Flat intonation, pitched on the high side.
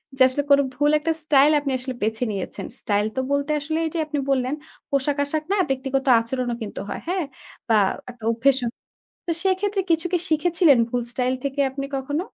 No: average, 3.4 semitones; very high, 275 Hz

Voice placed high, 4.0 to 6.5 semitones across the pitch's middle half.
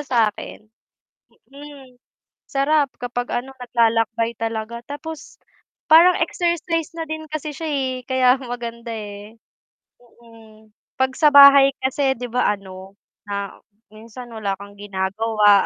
Yes: high, 245 Hz; average, 4.3 semitones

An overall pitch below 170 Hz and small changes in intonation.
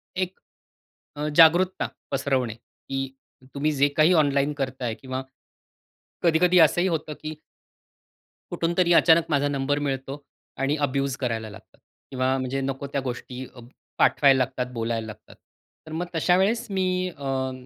No: medium, 140 Hz; average, 3.7 semitones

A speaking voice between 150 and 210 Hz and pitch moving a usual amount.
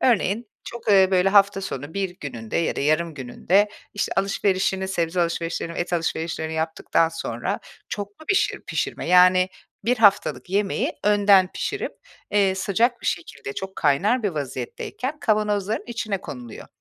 Yes: high, 190 Hz; average, 3.8 semitones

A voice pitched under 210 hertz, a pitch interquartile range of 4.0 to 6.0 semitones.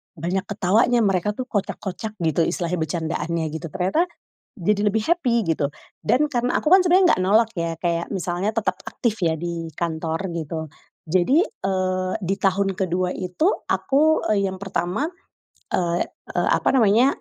Yes: high, 190 Hz; average, 4.5 semitones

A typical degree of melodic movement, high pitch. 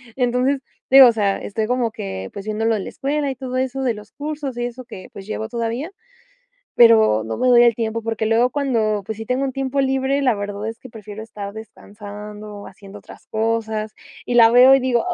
Yes: average, 3.5 semitones; high, 230 Hz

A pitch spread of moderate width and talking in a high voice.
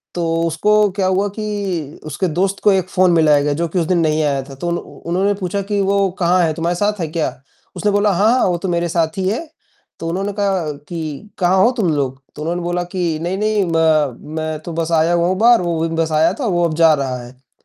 No: average, 3.3 semitones; medium, 175 Hz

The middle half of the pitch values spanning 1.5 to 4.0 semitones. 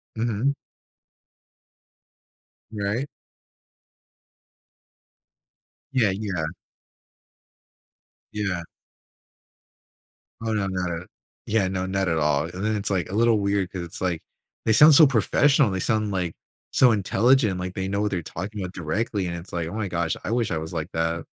Yes: average, 3.6 semitones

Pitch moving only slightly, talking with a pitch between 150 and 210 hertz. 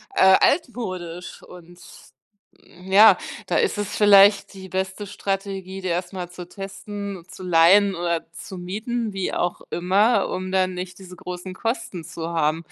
Yes: narrow, 2.2 semitones; high, 190 Hz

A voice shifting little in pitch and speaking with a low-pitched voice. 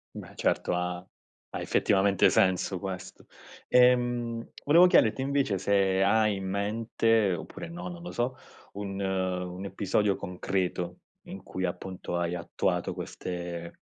No: average, 4.0 semitones; very low, 95 Hz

